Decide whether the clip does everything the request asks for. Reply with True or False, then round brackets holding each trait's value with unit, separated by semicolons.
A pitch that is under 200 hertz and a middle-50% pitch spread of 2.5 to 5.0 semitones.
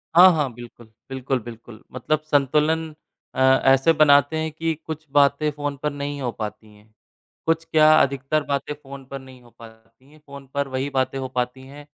True (140 Hz; 2.8 semitones)